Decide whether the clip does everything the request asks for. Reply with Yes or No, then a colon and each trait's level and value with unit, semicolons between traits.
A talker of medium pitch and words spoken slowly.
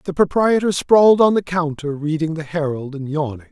No: medium, 165 Hz; average, 190 wpm